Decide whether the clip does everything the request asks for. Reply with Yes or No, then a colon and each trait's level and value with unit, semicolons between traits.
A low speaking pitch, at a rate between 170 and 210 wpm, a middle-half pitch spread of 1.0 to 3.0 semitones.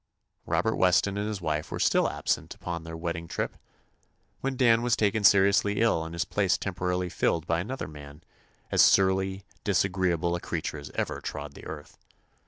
No: very low, 90 Hz; average, 180 wpm; average, 3.5 semitones